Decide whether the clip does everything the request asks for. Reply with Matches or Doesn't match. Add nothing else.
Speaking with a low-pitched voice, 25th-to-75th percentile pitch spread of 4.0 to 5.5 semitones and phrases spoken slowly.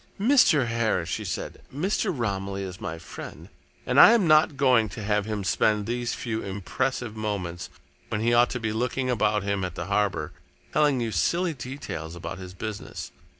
Doesn't match